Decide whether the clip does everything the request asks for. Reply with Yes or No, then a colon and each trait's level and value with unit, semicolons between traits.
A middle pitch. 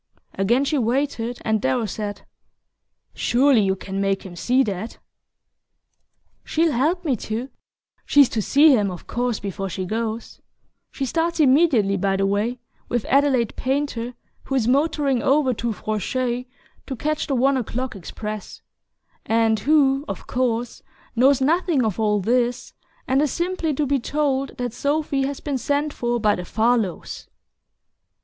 No: high, 245 Hz